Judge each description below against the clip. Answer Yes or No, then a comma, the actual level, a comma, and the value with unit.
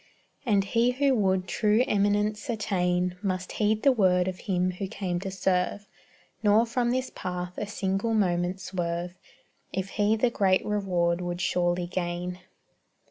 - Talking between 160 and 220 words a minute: No, average, 150 wpm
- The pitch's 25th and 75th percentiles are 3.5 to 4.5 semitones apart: No, average, 2.9 semitones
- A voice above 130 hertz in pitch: Yes, high, 190 Hz